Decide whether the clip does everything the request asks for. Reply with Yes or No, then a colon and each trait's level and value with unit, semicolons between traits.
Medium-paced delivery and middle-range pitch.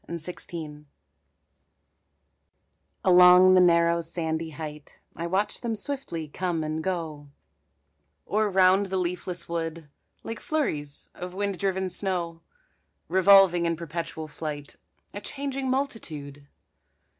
No: slow, 110 wpm; medium, 175 Hz